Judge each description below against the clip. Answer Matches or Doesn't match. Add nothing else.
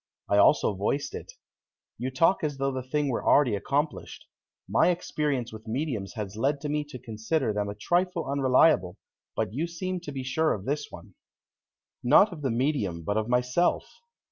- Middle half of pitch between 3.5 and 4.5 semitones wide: Doesn't match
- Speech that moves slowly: Doesn't match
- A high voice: Doesn't match